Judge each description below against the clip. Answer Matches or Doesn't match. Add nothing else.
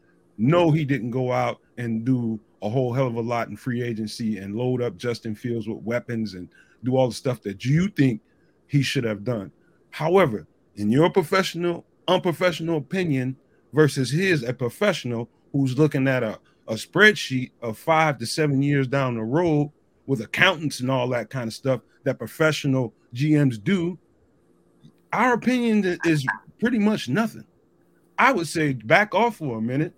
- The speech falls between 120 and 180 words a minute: Matches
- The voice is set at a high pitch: Doesn't match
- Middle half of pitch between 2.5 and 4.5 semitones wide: Doesn't match